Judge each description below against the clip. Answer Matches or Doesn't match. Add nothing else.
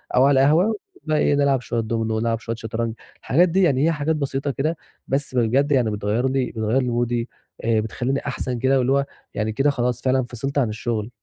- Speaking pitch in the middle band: Doesn't match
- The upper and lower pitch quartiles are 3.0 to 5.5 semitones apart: Matches